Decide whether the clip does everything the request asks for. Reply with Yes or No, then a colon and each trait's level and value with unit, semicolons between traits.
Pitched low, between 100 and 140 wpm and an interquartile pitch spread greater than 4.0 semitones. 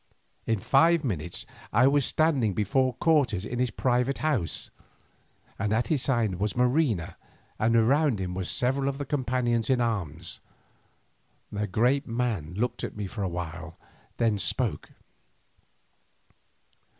Yes: low, 120 Hz; slow, 135 wpm; average, 4.9 semitones